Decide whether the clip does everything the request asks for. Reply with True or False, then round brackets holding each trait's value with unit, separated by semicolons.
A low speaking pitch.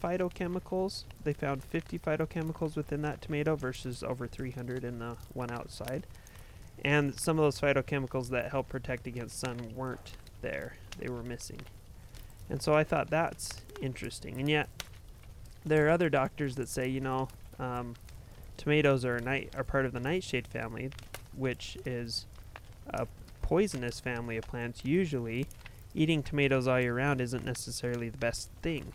True (130 Hz)